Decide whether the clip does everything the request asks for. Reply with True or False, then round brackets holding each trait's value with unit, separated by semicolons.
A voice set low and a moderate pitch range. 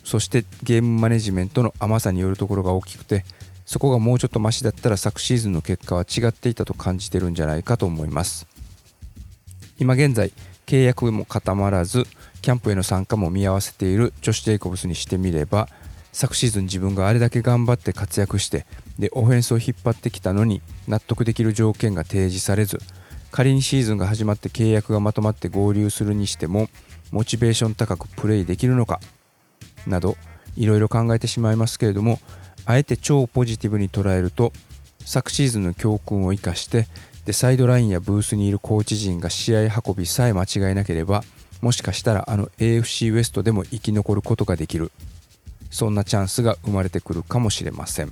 True (105 Hz; 3.7 semitones)